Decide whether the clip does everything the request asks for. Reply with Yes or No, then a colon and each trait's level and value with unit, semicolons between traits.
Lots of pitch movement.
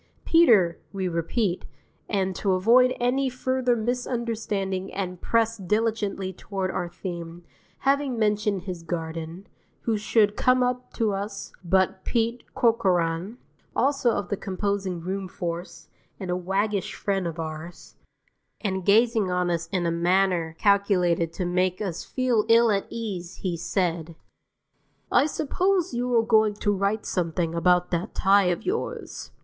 No: average, 4.2 semitones